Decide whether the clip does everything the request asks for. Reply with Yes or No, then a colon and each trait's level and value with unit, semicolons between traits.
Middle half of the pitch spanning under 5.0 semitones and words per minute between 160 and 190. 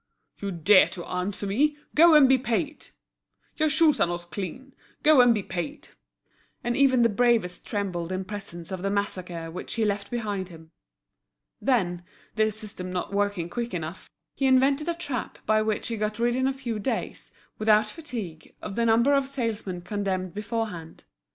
No: wide, 5.4 semitones; average, 175 wpm